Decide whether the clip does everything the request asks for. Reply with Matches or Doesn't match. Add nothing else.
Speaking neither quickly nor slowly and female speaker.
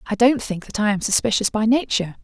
Doesn't match